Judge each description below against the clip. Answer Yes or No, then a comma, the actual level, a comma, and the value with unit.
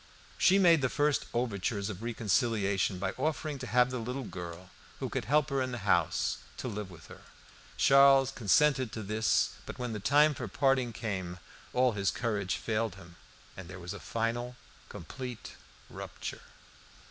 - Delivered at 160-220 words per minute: Yes, average, 170 wpm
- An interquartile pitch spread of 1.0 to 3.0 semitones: No, average, 4.9 semitones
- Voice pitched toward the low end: Yes, low, 115 Hz